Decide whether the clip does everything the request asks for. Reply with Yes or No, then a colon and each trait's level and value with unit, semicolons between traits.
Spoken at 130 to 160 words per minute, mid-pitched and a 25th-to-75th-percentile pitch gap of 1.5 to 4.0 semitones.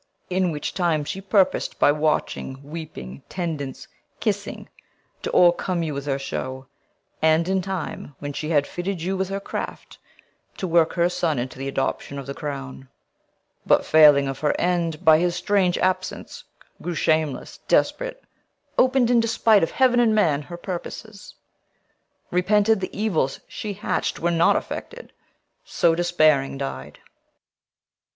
No: average, 145 wpm; medium, 170 Hz; average, 4.7 semitones